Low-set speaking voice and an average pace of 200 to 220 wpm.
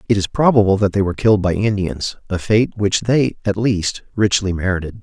Yes: low, 100 Hz; fast, 205 wpm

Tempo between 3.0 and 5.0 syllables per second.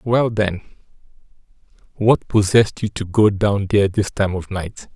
Yes: 4.6 syllables/s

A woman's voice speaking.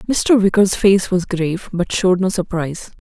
Yes: female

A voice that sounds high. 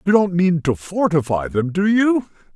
No: medium, 170 Hz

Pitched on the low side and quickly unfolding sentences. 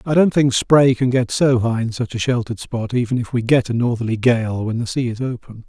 Yes: low, 120 Hz; fast, 265 wpm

